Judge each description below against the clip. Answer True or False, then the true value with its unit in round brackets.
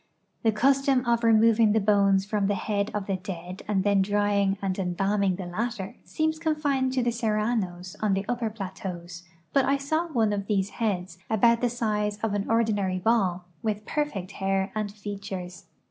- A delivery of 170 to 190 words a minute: True (185 wpm)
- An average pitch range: True (3.1 semitones)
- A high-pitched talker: True (205 Hz)